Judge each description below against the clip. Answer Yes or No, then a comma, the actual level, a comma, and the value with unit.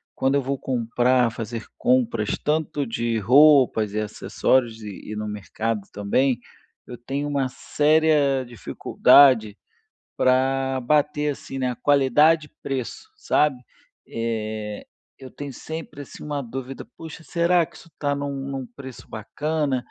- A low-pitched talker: Yes, low, 130 Hz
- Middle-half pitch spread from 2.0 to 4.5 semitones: Yes, average, 3.9 semitones